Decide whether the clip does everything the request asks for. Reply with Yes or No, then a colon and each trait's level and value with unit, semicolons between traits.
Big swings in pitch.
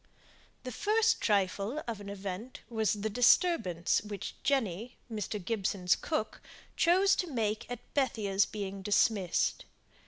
No: average, 4.2 semitones